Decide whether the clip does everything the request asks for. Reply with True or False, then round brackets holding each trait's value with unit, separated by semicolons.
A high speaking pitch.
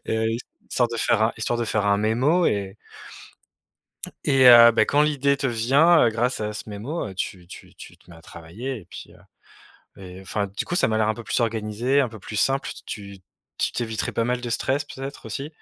False (115 Hz)